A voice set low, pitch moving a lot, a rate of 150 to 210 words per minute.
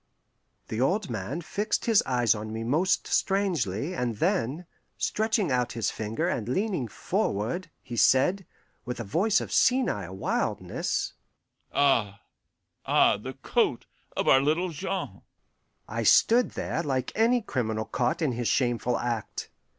No: low, 130 Hz; wide, 8.6 semitones; average, 140 wpm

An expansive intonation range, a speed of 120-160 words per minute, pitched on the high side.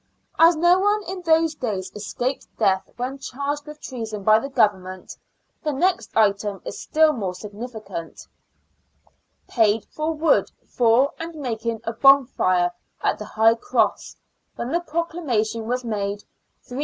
Yes: wide, 6.3 semitones; average, 150 wpm; high, 245 Hz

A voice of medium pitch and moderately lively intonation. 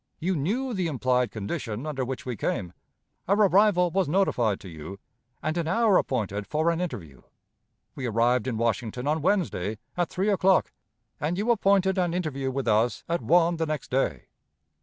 No: medium, 155 Hz; wide, 7.3 semitones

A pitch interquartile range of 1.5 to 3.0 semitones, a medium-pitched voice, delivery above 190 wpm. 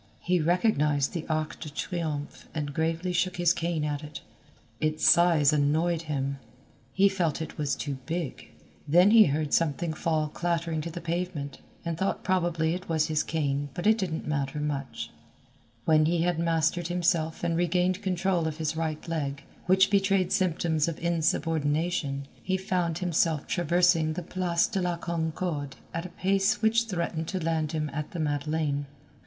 No: narrow, 2.5 semitones; medium, 165 Hz; average, 165 wpm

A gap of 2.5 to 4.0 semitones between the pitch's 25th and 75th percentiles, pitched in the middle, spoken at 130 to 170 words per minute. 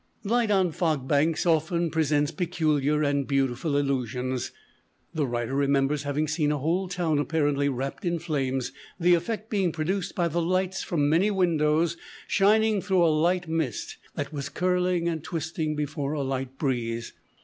Yes: average, 3.7 semitones; medium, 155 Hz; average, 160 wpm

